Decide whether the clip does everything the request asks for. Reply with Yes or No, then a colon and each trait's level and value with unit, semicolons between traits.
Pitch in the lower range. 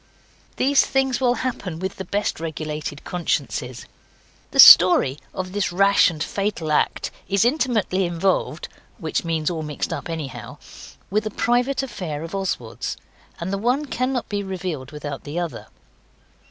No: medium, 185 Hz